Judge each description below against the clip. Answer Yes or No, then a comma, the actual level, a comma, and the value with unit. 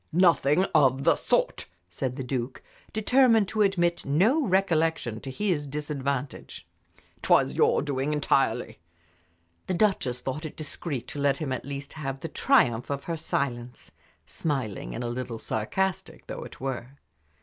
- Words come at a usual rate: Yes, average, 150 wpm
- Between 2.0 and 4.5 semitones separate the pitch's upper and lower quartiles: No, average, 4.9 semitones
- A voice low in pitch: No, medium, 145 Hz